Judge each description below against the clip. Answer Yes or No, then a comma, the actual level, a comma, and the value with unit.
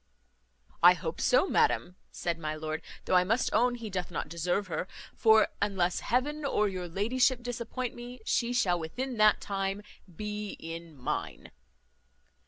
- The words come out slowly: No, average, 155 wpm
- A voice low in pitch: No, high, 200 Hz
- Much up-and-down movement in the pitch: Yes, wide, 5.7 semitones